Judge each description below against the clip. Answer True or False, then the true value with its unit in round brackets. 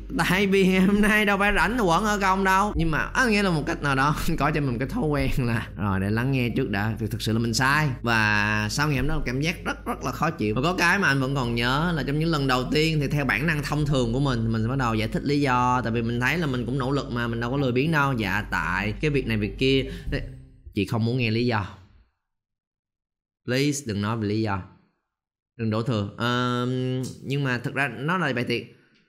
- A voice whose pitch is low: True (130 Hz)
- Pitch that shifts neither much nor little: True (4.8 semitones)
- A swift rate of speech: True (265 wpm)